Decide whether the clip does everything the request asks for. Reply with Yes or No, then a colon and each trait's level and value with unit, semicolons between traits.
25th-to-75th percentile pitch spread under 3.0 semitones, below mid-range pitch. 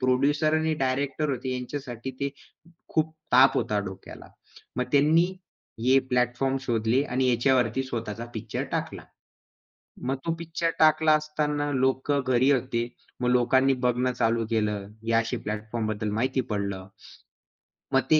No: average, 3.4 semitones; low, 130 Hz